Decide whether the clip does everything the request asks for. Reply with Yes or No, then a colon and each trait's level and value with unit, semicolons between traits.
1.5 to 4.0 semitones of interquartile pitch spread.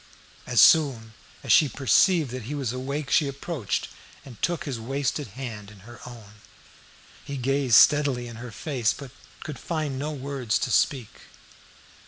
Yes: average, 3.4 semitones